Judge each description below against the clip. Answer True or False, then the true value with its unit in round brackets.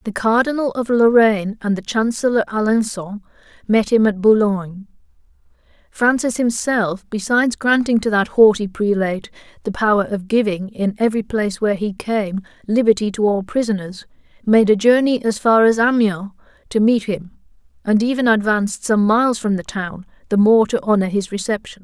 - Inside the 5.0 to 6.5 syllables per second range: True (5.3 syllables/s)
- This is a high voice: True (215 Hz)